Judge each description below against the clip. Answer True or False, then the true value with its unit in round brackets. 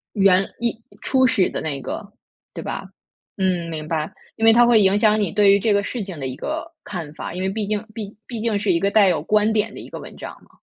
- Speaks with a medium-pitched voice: False (200 Hz)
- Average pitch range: True (3.4 semitones)